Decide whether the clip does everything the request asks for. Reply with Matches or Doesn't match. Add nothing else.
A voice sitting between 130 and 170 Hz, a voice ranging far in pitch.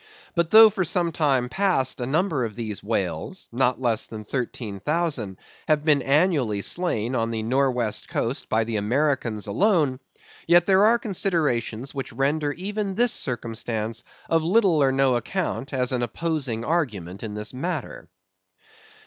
Matches